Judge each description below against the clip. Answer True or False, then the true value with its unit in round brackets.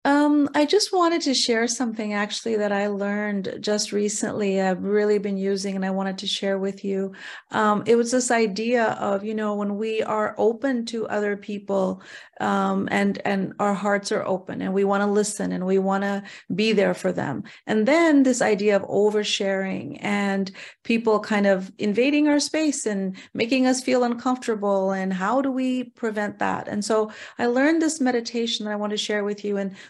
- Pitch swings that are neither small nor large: True (3.2 semitones)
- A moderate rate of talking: True (195 wpm)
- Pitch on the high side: True (210 Hz)